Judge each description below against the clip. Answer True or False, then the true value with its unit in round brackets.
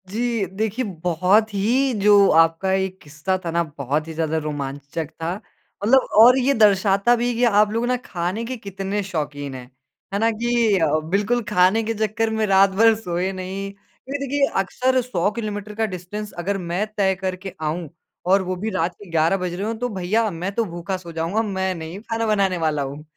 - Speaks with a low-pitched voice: False (195 Hz)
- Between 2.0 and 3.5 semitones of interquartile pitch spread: False (4.3 semitones)